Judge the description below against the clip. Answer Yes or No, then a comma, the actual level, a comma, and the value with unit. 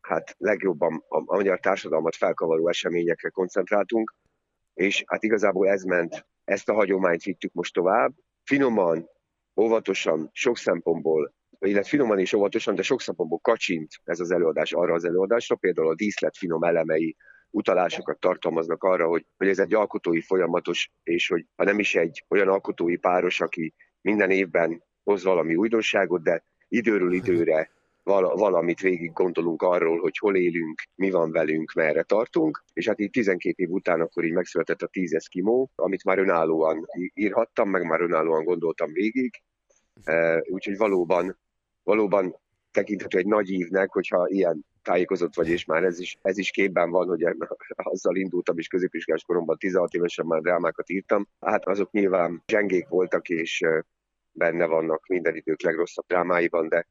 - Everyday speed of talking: No, fast, 160 wpm